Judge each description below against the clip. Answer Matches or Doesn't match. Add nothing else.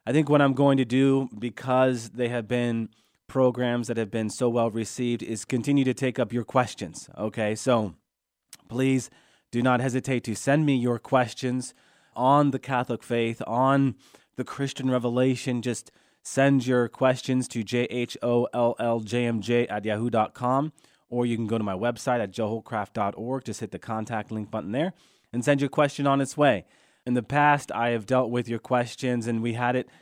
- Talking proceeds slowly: Doesn't match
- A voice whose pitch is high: Doesn't match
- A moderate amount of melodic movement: Doesn't match